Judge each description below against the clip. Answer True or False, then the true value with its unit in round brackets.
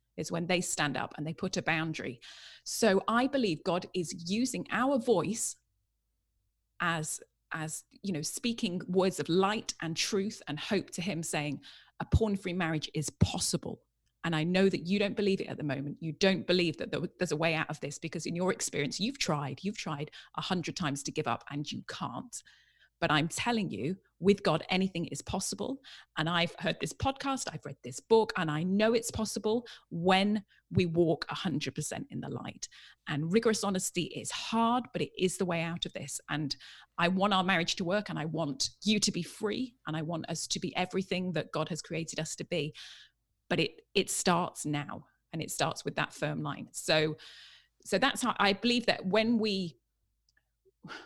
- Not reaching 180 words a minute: False (195 wpm)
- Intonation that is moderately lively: True (4.6 semitones)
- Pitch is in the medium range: True (175 Hz)